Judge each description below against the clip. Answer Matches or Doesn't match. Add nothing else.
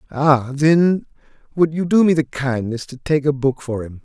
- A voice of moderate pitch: Matches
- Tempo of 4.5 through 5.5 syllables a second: Matches